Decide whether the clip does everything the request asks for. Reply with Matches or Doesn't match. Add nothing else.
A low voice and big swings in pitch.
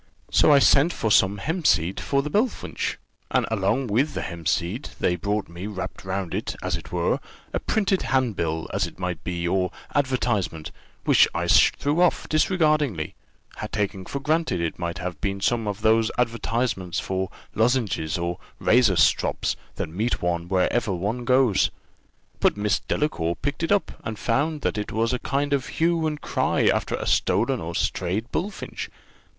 Matches